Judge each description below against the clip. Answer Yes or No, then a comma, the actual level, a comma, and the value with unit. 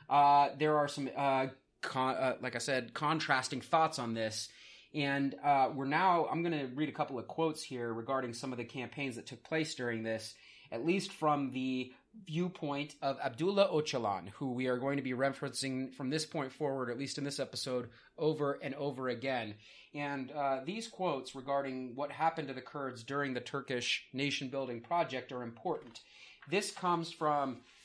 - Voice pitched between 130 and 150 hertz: Yes, low, 135 Hz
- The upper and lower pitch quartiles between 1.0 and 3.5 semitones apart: Yes, average, 2.8 semitones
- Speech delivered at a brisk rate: No, average, 185 wpm